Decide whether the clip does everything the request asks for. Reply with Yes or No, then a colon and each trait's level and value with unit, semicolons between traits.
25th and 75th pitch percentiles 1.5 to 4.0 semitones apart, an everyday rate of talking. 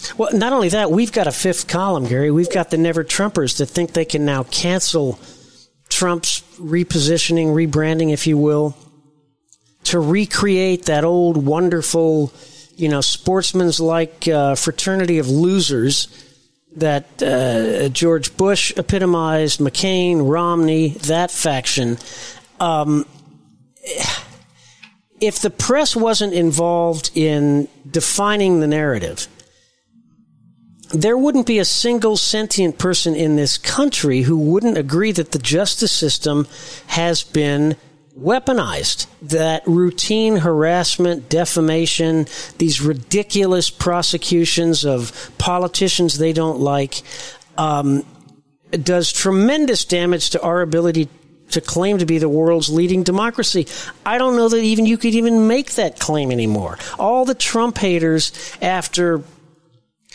No: average, 3.4 semitones; slow, 120 wpm